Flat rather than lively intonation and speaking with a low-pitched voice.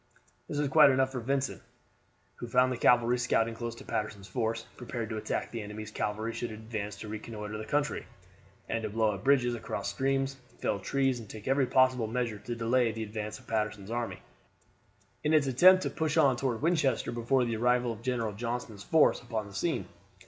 No: average, 3.2 semitones; low, 120 Hz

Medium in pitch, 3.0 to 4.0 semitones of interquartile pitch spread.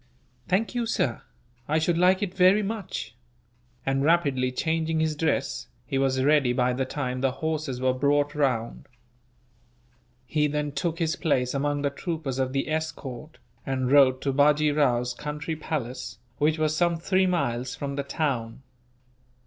Yes: medium, 145 Hz; average, 3.5 semitones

